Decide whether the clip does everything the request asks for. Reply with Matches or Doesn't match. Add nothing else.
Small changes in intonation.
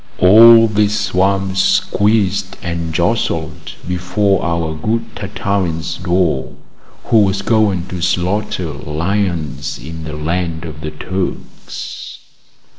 Doesn't match